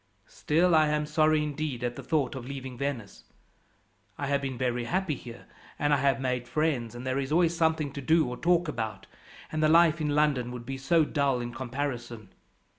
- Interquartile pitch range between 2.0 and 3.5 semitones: No, average, 3.9 semitones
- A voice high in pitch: No, medium, 140 Hz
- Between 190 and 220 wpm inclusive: Yes, average, 200 wpm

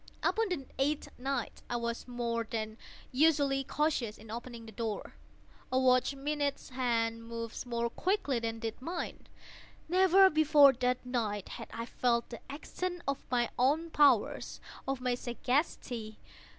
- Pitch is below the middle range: No, very high, 250 Hz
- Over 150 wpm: No, average, 140 wpm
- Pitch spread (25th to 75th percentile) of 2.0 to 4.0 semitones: Yes, average, 3.7 semitones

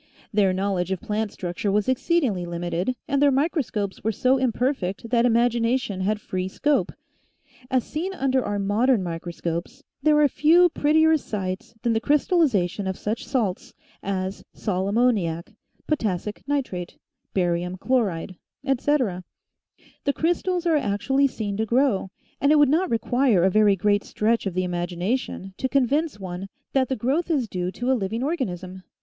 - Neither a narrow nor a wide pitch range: No, wide, 6.3 semitones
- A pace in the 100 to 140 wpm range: No, average, 160 wpm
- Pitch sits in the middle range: No, high, 220 Hz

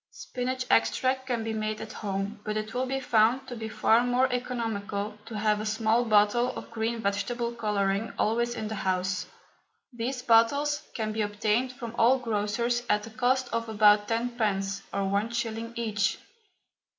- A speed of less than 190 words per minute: Yes, average, 170 wpm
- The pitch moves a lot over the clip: No, narrow, 2.5 semitones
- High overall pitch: Yes, high, 225 Hz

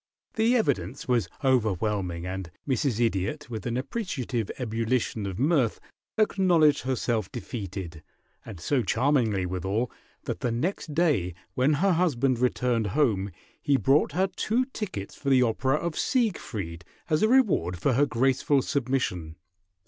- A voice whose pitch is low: Yes, low, 125 Hz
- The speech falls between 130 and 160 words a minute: Yes, average, 140 wpm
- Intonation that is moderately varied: No, wide, 6.6 semitones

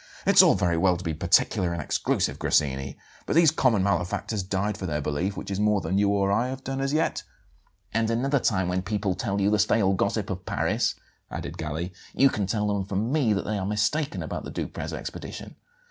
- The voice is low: Yes, low, 100 Hz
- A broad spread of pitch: No, average, 3.5 semitones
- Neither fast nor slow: No, fast, 215 wpm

